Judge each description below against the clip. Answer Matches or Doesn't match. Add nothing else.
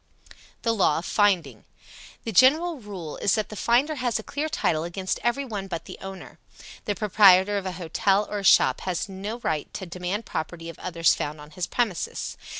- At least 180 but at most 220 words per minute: Matches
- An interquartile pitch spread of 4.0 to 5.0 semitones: Matches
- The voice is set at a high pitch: Matches